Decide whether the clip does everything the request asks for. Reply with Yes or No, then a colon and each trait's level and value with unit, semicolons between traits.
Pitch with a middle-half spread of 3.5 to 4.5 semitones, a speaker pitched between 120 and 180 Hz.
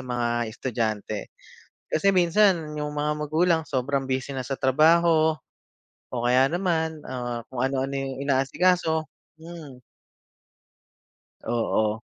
Yes: average, 4.2 semitones; medium, 140 Hz